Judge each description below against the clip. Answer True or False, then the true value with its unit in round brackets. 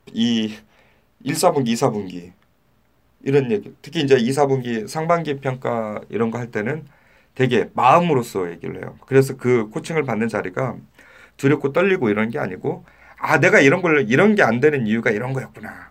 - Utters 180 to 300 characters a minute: False (315 characters per minute)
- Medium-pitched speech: False (125 Hz)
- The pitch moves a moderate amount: True (4.4 semitones)